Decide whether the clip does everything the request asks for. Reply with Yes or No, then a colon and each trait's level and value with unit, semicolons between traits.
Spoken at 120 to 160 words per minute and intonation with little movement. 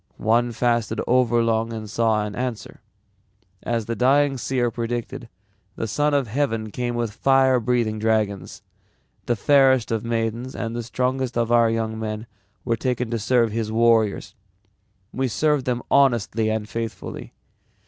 Yes: average, 150 wpm; narrow, 2.1 semitones